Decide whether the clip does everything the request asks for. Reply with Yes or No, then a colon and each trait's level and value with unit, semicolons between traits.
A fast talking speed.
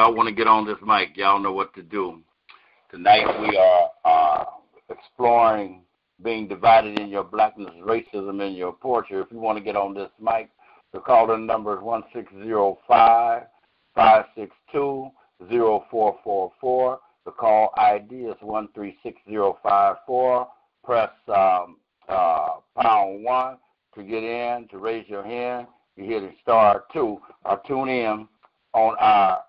No: average, 165 wpm